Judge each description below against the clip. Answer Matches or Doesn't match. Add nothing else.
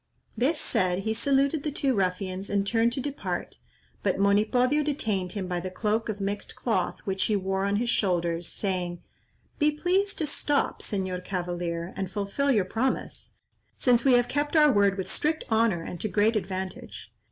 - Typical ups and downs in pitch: Doesn't match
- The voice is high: Matches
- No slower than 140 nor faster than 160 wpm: Doesn't match